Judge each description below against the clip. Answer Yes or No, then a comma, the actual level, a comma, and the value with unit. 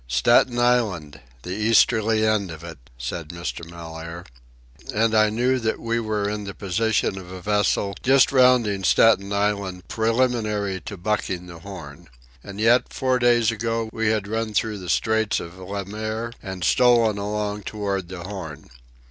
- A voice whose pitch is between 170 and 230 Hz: No, low, 105 Hz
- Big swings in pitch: No, average, 3.4 semitones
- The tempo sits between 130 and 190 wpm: Yes, average, 160 wpm